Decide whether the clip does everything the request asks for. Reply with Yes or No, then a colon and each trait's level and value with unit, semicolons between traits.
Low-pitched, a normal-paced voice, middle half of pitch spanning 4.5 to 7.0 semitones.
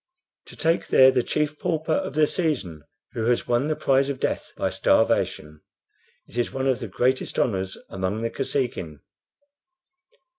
Yes: low, 130 Hz; average, 160 wpm; average, 5.0 semitones